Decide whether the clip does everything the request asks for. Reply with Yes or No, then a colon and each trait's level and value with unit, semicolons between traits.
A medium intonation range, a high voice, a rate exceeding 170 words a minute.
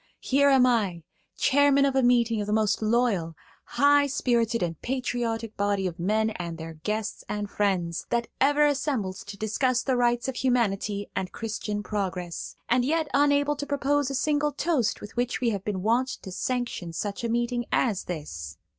Yes: average, 4.7 semitones; high, 230 Hz; average, 180 wpm